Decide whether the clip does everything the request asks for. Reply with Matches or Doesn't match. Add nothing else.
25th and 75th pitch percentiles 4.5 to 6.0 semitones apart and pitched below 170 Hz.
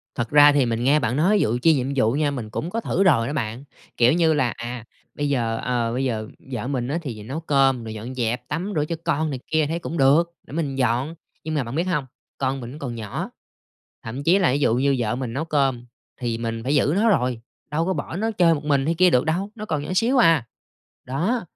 Matches